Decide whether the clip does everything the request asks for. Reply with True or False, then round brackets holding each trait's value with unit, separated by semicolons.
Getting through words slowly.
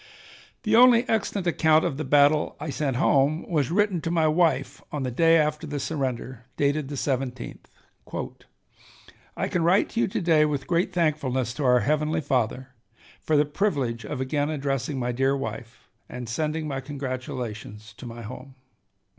False (170 wpm)